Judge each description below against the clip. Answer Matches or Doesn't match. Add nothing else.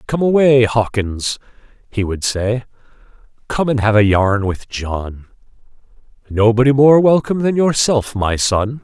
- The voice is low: Matches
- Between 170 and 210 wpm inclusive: Doesn't match